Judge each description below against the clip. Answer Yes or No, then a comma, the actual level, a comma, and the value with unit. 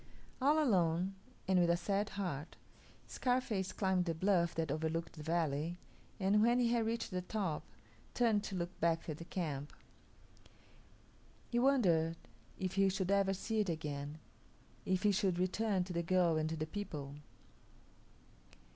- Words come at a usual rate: Yes, average, 155 wpm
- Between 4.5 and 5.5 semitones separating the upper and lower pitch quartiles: No, average, 3.8 semitones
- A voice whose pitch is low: No, medium, 180 Hz